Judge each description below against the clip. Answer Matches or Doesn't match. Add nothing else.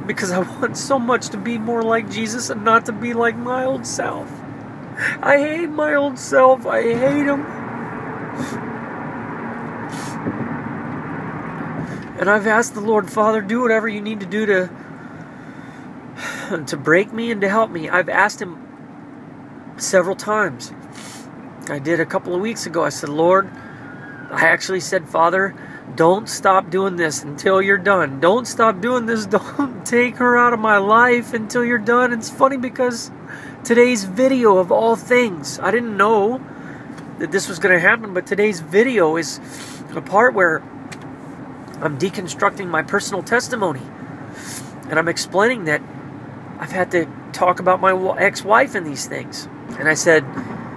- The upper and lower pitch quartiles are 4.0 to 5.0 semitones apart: Matches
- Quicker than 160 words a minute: Doesn't match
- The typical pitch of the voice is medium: Doesn't match